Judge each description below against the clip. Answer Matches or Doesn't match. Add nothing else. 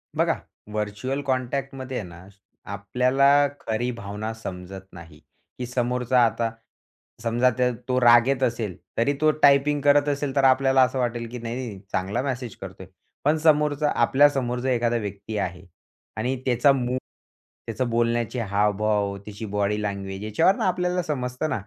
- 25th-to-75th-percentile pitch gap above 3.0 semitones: Matches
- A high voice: Doesn't match